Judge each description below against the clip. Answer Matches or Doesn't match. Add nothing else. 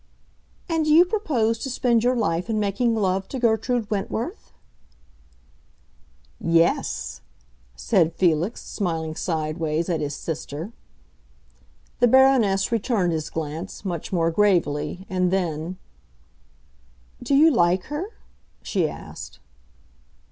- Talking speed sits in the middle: Doesn't match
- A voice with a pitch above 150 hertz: Matches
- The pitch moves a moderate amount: Doesn't match